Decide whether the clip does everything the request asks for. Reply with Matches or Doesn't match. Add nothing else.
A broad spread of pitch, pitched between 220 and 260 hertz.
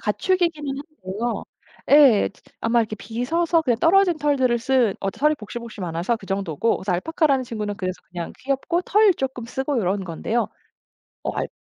Matches